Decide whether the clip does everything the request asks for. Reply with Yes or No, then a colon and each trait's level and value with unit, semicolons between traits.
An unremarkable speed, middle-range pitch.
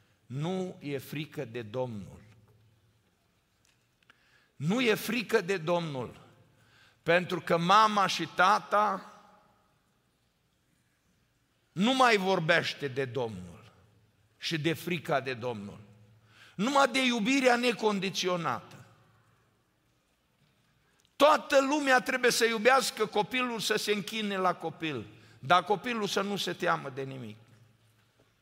No: slow, 100 wpm; medium, 175 Hz